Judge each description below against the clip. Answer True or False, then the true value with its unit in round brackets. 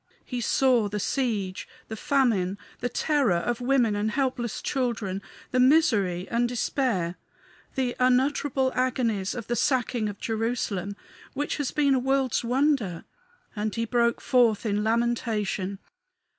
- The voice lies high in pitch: True (235 Hz)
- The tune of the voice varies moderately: True (3.8 semitones)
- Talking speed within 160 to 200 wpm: False (135 wpm)